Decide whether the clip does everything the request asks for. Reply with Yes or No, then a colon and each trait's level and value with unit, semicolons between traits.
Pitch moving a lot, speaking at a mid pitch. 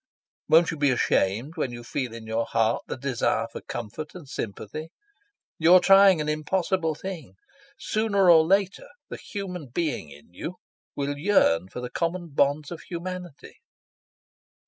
Yes: wide, 6.9 semitones; medium, 155 Hz